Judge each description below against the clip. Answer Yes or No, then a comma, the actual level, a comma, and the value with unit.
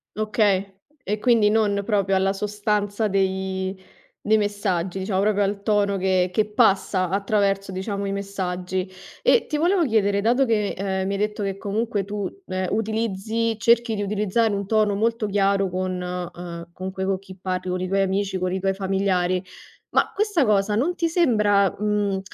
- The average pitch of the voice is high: Yes, high, 200 Hz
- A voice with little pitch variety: Yes, narrow, 2.0 semitones